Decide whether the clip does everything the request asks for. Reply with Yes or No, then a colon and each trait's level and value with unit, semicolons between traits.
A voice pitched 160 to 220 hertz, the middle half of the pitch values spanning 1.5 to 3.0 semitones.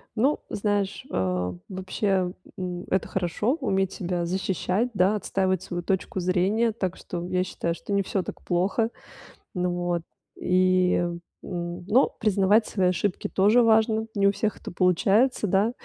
Yes: high, 190 Hz; narrow, 2.6 semitones